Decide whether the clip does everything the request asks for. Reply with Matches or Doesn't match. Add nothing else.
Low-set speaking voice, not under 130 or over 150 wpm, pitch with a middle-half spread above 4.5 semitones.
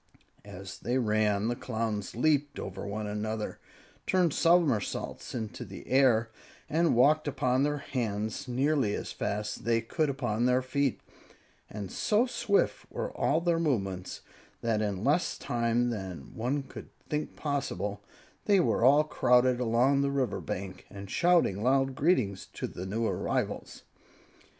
Matches